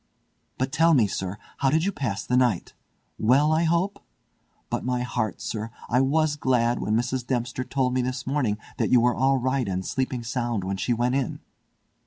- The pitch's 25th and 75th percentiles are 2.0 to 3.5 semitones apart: Yes, narrow, 2.5 semitones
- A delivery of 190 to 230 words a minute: Yes, average, 195 wpm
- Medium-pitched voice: No, low, 125 Hz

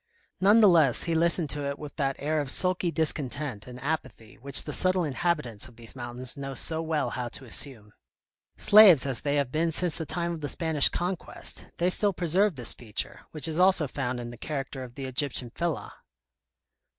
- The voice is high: No, medium, 145 Hz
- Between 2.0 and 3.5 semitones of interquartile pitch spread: No, average, 4.7 semitones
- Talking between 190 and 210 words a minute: Yes, average, 200 wpm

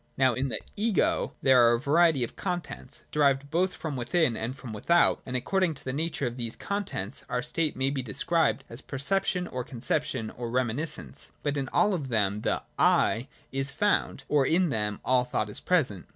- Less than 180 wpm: No, fast, 205 wpm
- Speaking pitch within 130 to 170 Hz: Yes, low, 135 Hz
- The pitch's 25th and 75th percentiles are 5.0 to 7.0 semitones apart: Yes, average, 5.3 semitones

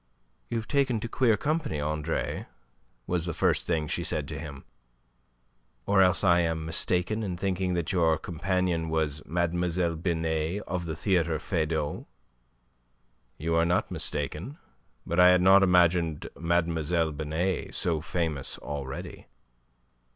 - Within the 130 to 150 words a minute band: Yes, slow, 135 wpm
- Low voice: Yes, very low, 85 Hz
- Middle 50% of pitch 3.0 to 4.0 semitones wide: No, narrow, 2.5 semitones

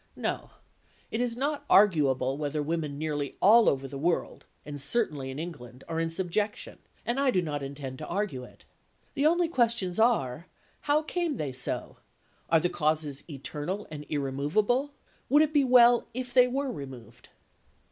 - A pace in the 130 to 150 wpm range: No, average, 165 wpm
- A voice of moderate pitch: Yes, medium, 170 Hz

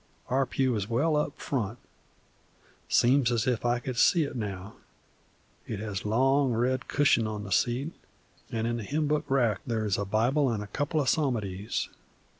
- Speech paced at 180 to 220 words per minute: Yes, average, 190 wpm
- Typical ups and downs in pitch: Yes, average, 4.0 semitones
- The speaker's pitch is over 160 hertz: No, low, 120 Hz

